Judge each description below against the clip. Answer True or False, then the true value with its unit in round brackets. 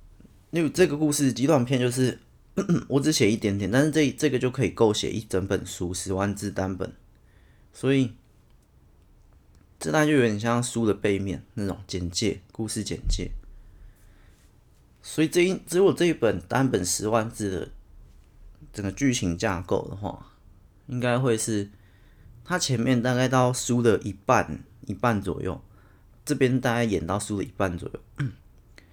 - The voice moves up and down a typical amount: True (4.9 semitones)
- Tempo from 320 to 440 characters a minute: False (225 characters per minute)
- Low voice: True (110 Hz)